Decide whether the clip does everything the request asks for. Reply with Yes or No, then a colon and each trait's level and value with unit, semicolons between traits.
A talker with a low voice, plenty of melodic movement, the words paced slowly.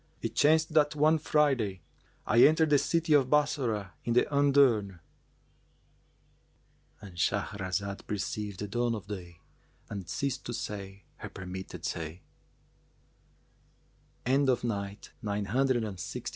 Yes: low, 110 Hz; wide, 6.7 semitones; slow, 100 wpm